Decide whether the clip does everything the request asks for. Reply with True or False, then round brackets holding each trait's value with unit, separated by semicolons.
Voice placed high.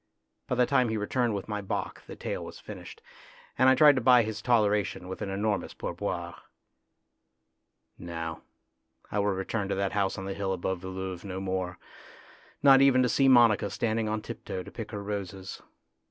False (105 Hz)